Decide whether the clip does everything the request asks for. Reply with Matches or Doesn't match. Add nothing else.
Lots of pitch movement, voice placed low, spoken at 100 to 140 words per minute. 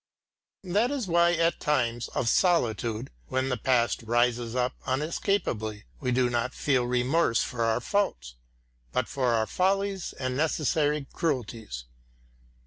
Matches